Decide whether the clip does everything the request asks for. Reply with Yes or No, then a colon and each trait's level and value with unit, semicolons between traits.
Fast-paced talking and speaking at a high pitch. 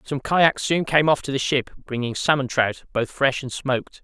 No: fast, 225 wpm; low, 135 Hz